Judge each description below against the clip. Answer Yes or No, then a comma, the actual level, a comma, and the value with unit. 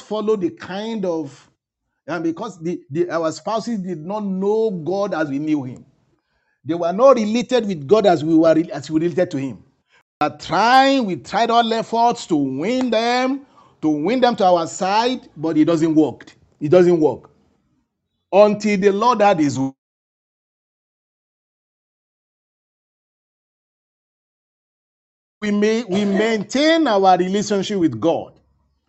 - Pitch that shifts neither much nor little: No, wide, 5.8 semitones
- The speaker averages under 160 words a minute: Yes, average, 140 wpm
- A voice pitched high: Yes, high, 195 Hz